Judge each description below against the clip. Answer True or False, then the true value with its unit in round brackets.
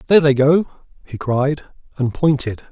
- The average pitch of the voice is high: False (140 Hz)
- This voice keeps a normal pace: True (155 wpm)